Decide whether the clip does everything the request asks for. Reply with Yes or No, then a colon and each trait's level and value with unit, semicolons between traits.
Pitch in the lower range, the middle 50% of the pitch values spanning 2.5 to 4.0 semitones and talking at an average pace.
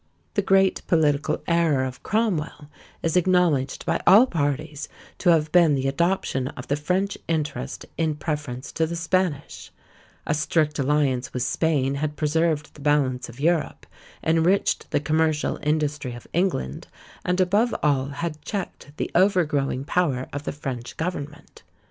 No: medium, 150 Hz; average, 3.3 semitones; average, 150 wpm